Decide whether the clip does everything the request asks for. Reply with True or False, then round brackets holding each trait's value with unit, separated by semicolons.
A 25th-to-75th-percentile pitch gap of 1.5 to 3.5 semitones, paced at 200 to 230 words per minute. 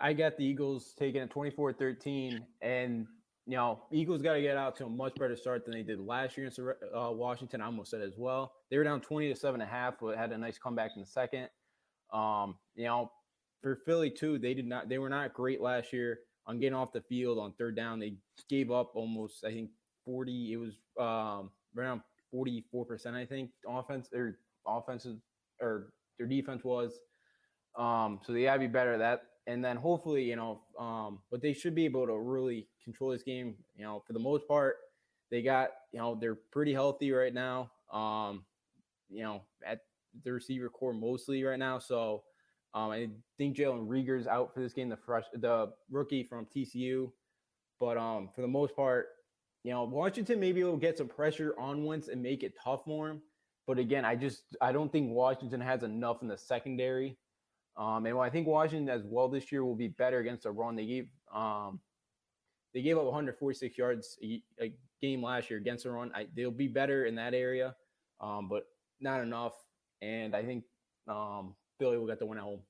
True (2.8 semitones; 205 wpm)